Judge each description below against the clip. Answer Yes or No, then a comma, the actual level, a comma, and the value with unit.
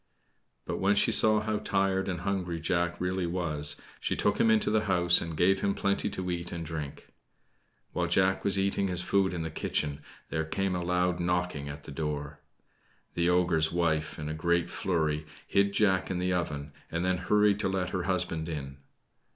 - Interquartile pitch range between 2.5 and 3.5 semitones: Yes, average, 2.9 semitones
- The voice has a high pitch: No, very low, 90 Hz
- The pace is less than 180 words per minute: No, average, 190 wpm